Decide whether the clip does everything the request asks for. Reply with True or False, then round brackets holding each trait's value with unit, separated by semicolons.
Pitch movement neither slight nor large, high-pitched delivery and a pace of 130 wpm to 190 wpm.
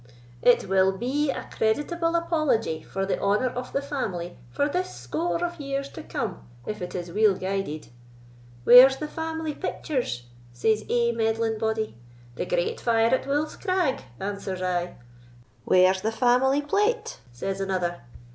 False (7.1 semitones; 225 Hz; 150 wpm)